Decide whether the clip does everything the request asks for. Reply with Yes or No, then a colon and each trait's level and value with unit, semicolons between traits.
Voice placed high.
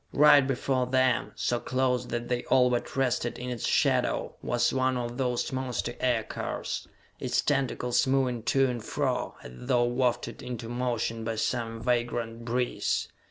No: low, 125 Hz